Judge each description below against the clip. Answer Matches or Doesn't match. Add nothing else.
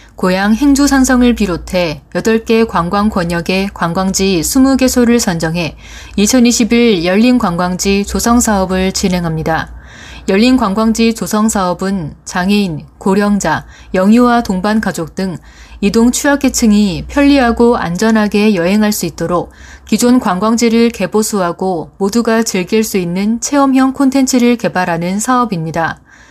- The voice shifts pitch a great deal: Doesn't match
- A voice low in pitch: Doesn't match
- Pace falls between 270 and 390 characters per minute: Matches